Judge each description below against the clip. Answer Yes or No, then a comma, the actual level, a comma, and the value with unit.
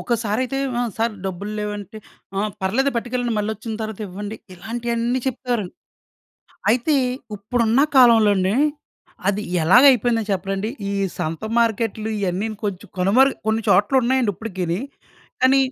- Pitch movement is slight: No, average, 3.2 semitones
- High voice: Yes, high, 220 Hz